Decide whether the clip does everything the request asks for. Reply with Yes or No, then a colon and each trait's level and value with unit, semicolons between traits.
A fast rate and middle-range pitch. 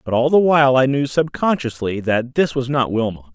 No: fast, 215 wpm; low, 130 Hz